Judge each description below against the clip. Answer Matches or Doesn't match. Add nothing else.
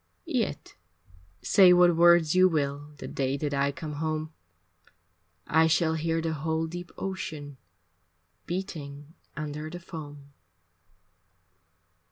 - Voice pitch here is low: Doesn't match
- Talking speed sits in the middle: Doesn't match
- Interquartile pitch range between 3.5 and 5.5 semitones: Doesn't match